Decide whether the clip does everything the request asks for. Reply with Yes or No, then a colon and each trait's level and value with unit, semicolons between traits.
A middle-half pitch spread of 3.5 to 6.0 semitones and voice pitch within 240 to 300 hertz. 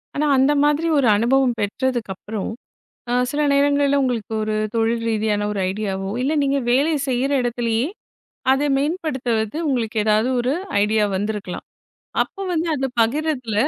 Yes: average, 4.4 semitones; high, 245 Hz